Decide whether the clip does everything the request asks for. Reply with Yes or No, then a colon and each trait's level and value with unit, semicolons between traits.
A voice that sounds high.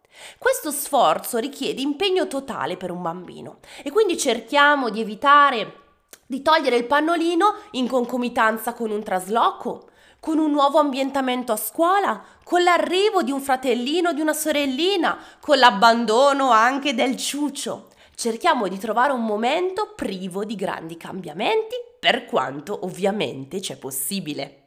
Yes: very high, 260 Hz